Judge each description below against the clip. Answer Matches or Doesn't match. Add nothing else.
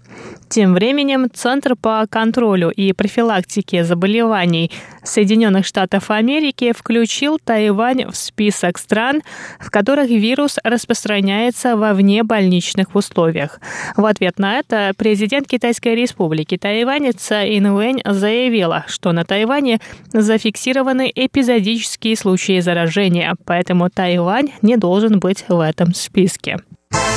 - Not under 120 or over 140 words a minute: Doesn't match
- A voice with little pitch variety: Doesn't match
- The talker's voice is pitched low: Doesn't match